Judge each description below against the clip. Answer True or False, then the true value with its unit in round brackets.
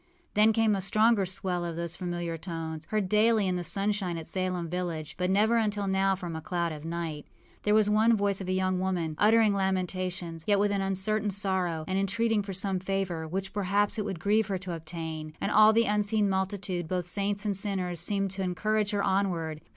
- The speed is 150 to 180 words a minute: False (205 wpm)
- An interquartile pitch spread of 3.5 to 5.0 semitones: False (2.8 semitones)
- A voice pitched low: False (190 Hz)